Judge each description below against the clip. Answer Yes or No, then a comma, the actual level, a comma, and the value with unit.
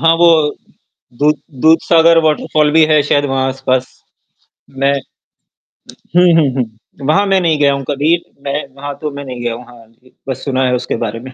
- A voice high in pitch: No, medium, 140 Hz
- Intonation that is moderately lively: Yes, average, 3.3 semitones